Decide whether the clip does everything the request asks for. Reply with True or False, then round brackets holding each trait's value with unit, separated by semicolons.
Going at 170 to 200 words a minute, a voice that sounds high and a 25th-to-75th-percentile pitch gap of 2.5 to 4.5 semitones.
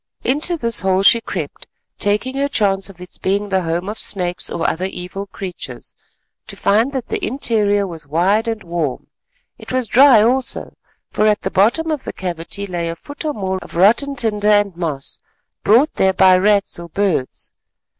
True (185 wpm; 200 Hz; 4.2 semitones)